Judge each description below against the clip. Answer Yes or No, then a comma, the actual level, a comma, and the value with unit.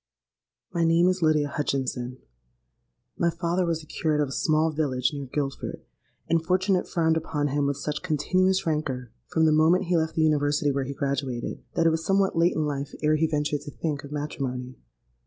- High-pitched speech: No, medium, 155 Hz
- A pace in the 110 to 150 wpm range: No, average, 195 wpm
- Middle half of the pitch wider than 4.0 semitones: No, average, 2.8 semitones